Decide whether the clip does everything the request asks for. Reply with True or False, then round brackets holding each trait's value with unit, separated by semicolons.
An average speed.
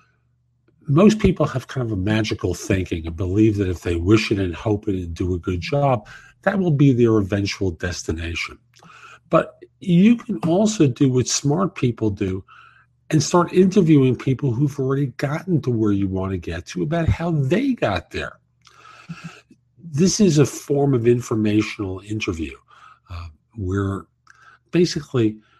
True (155 wpm)